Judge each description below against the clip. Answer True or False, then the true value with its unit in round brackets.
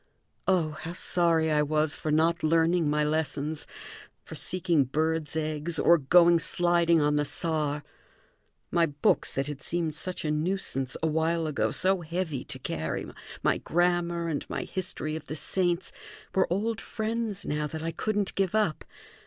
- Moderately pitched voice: True (160 Hz)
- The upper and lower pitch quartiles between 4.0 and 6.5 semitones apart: False (2.5 semitones)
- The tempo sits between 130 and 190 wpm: True (160 wpm)